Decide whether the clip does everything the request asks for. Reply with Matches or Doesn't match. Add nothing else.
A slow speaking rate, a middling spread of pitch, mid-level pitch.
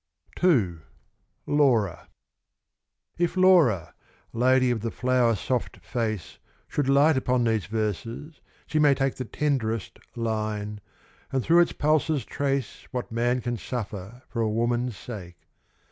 Doesn't match